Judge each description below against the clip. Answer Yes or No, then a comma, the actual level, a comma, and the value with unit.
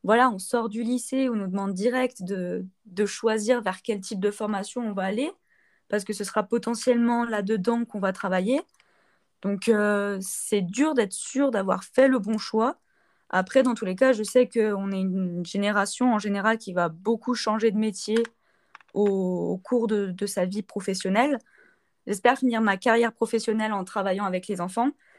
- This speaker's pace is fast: No, average, 185 wpm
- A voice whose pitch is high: Yes, high, 215 Hz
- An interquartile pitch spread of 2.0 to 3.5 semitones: Yes, average, 3.2 semitones